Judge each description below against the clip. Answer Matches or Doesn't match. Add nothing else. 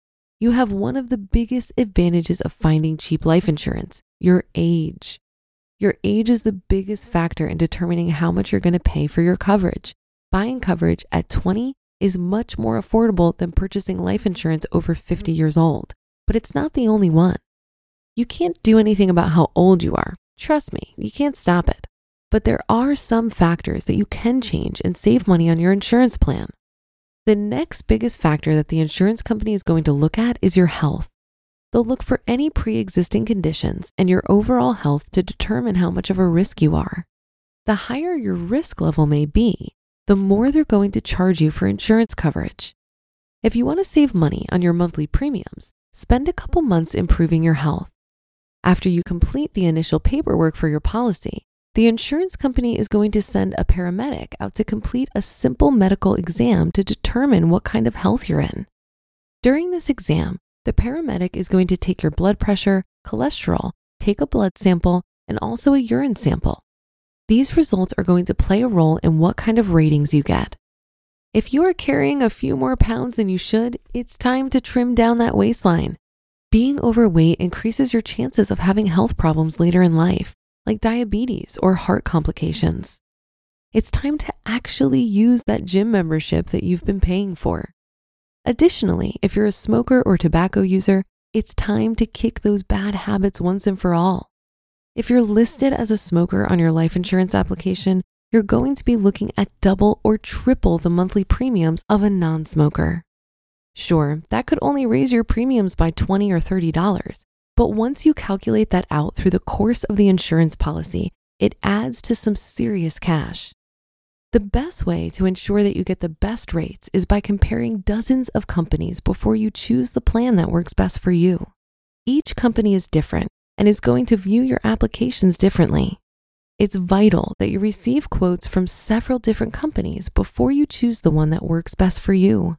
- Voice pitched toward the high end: Matches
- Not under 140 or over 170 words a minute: Doesn't match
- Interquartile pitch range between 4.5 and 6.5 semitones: Matches